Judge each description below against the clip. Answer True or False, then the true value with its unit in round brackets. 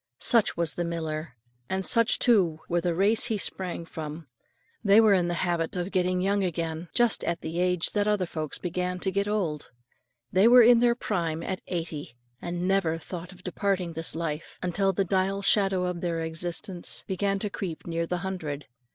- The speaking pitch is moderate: True (180 Hz)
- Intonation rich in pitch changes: False (2.8 semitones)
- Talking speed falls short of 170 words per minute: False (190 wpm)